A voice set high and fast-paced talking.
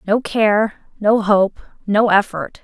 No: high, 210 Hz; slow, 90 wpm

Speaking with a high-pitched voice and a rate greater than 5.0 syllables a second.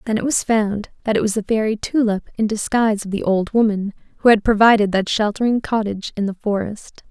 Yes: high, 215 Hz; 5.9 syllables/s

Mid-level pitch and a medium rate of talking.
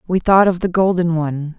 No: medium, 175 Hz; fast, 225 wpm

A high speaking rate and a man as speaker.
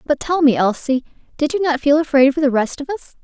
No: fast, 260 wpm; female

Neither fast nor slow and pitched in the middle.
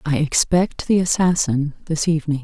Yes: average, 150 wpm; medium, 160 Hz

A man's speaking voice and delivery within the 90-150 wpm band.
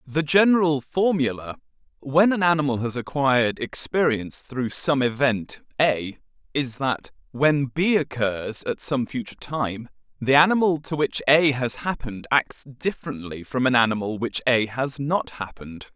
Yes: male; average, 145 wpm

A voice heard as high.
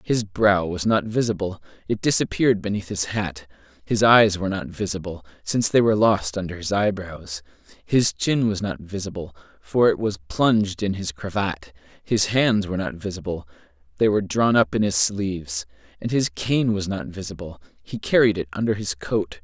No: very low, 95 Hz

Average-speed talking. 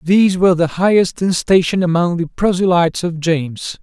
Yes: average, 175 wpm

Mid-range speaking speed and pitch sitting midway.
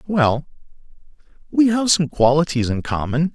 No: slow, 125 wpm; medium, 155 Hz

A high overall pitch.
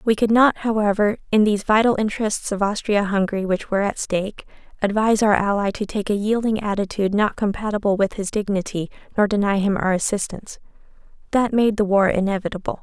Yes: high, 205 Hz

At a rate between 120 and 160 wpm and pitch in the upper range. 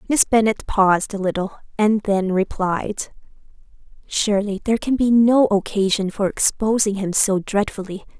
Yes: average, 140 wpm; high, 205 Hz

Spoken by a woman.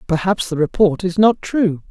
Yes: female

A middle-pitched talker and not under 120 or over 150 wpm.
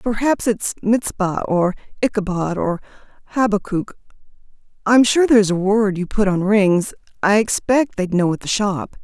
No: high, 205 Hz; average, 145 wpm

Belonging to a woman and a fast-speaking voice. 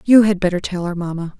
Yes: female; fast, 260 wpm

